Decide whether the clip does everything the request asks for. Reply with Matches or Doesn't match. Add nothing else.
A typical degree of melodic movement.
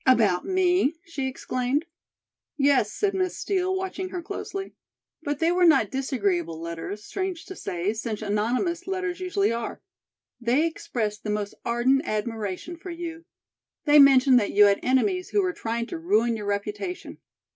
Doesn't match